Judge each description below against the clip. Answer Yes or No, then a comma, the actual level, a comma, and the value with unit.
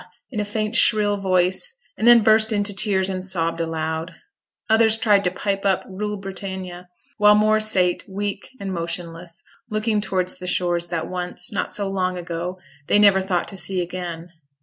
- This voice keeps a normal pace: Yes, average, 170 wpm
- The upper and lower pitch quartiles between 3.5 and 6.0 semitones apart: No, average, 2.7 semitones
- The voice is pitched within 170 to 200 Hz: Yes, high, 190 Hz